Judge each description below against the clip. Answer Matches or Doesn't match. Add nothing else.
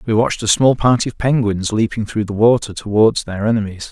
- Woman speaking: Doesn't match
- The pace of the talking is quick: Matches